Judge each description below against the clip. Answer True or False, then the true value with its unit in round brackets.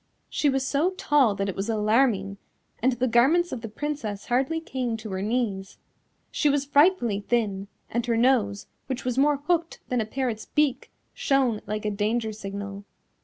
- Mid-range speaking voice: False (240 Hz)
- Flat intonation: False (4.6 semitones)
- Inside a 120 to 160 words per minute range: False (175 wpm)